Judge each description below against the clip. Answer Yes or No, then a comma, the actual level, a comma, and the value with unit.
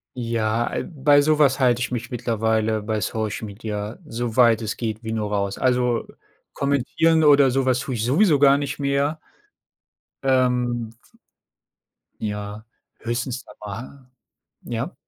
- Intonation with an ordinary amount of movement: Yes, average, 3.6 semitones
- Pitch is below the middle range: Yes, low, 120 Hz